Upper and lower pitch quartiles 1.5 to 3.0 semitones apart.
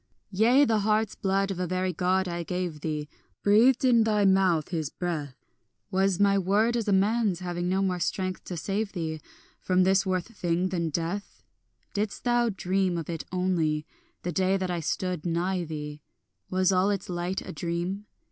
Yes: narrow, 2.4 semitones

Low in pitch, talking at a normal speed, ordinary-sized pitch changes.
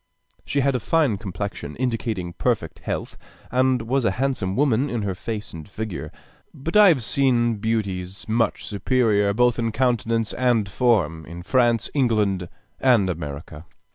Yes: low, 115 Hz; average, 150 wpm; average, 4.7 semitones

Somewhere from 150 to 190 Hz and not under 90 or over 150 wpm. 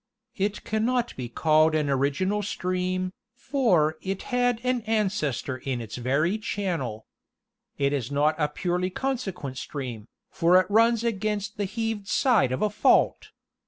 Yes: medium, 185 Hz; average, 145 wpm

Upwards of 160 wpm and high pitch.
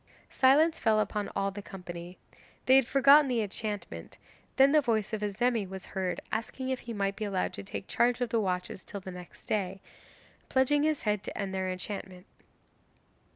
Yes: average, 185 wpm; high, 210 Hz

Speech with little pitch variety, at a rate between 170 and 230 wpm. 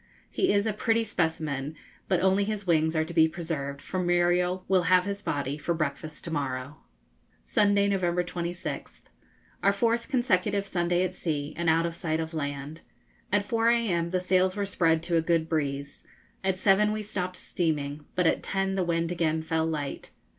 No: average, 3.3 semitones; average, 180 wpm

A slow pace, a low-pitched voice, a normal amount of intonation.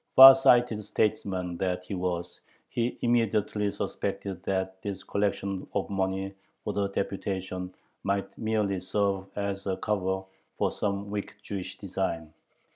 No: slow, 130 wpm; low, 100 Hz; narrow, 1.6 semitones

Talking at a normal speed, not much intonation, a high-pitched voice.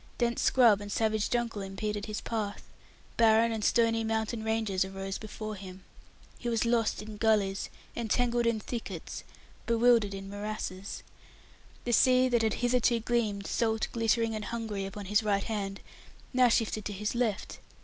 Yes: average, 155 wpm; narrow, 2.3 semitones; high, 220 Hz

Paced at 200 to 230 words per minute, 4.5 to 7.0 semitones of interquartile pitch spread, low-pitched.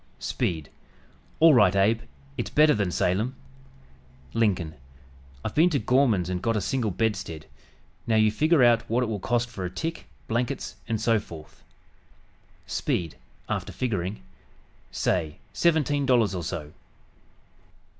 No: slow, 135 wpm; average, 5.3 semitones; low, 110 Hz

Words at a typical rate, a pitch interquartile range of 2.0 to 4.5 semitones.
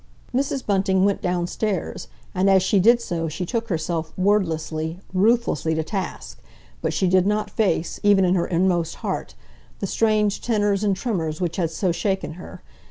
Yes: average, 160 wpm; average, 3.5 semitones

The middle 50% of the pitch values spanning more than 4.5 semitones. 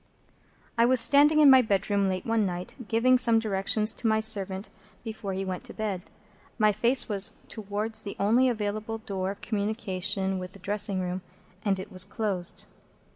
No: narrow, 2.6 semitones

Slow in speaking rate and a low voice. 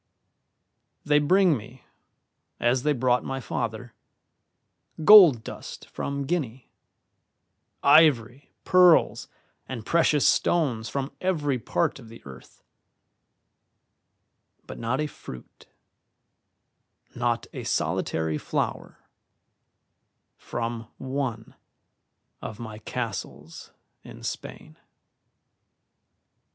Yes: slow, 85 wpm; low, 125 Hz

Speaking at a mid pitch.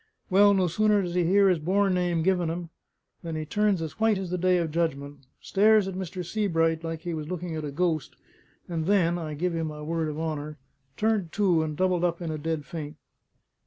Yes: medium, 170 Hz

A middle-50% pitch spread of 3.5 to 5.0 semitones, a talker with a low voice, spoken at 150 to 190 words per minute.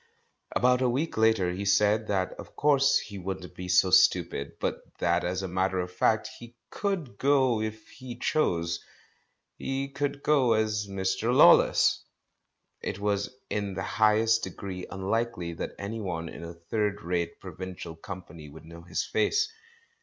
Yes: average, 4.6 semitones; low, 100 Hz; average, 160 wpm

